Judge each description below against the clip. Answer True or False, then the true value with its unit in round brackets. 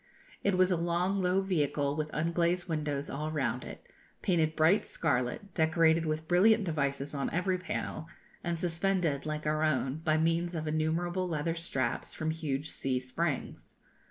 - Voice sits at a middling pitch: True (160 Hz)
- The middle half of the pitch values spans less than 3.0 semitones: True (2.5 semitones)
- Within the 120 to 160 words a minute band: True (155 wpm)